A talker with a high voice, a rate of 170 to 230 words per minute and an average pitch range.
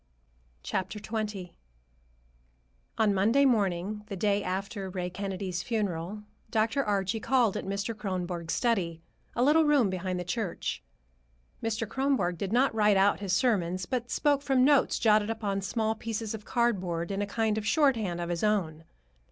No: high, 205 Hz; average, 150 wpm; average, 3.5 semitones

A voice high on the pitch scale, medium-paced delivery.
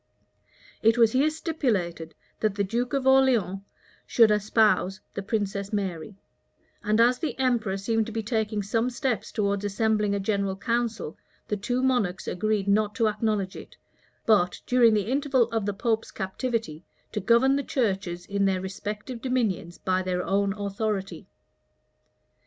Yes: high, 215 Hz; average, 150 wpm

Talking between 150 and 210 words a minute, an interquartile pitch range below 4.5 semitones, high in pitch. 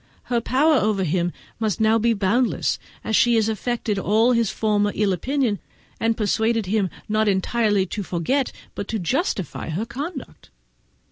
Yes: average, 160 wpm; average, 2.9 semitones; high, 220 Hz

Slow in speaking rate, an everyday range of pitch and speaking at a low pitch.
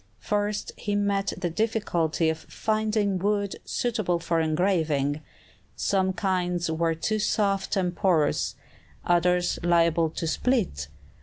No: slow, 120 wpm; average, 3.7 semitones; medium, 180 Hz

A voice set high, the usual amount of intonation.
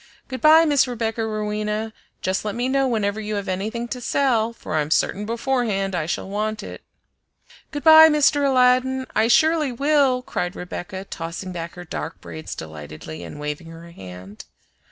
No: high, 215 Hz; wide, 6.6 semitones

